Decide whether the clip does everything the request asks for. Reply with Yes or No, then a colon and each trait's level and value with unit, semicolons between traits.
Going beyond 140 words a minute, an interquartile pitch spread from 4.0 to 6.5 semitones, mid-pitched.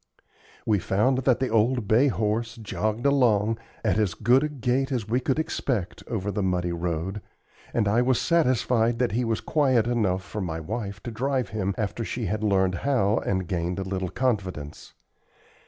No: average, 180 wpm; average, 4.3 semitones; low, 110 Hz